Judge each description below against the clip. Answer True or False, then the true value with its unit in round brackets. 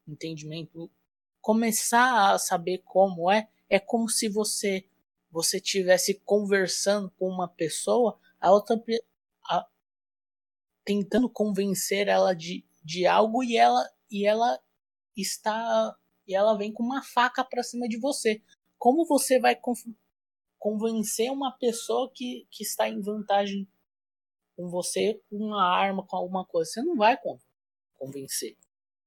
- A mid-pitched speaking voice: False (205 Hz)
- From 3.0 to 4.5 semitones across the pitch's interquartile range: True (3.8 semitones)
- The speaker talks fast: False (135 wpm)